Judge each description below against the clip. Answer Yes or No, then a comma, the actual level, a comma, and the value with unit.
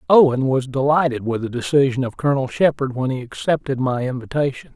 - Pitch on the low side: Yes, low, 130 Hz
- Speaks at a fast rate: No, average, 175 wpm